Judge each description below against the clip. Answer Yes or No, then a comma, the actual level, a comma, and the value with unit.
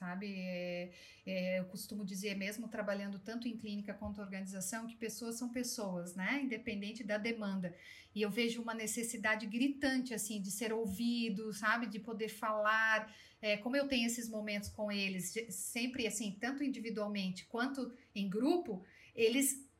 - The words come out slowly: Yes, slow, 155 wpm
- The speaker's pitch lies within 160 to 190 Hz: No, high, 220 Hz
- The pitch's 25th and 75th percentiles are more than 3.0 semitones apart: No, narrow, 2.5 semitones